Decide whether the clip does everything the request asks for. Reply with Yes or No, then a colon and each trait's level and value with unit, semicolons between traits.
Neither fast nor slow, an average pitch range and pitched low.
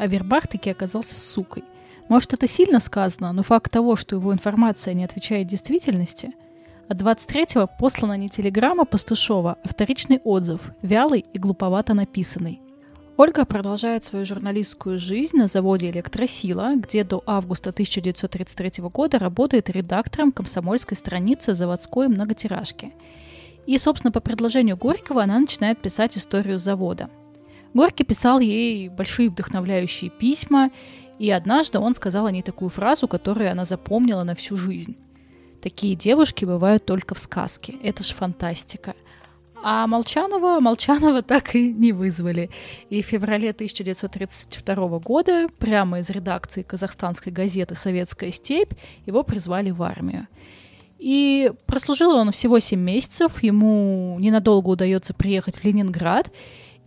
No: average, 130 wpm; average, 4.5 semitones; high, 205 Hz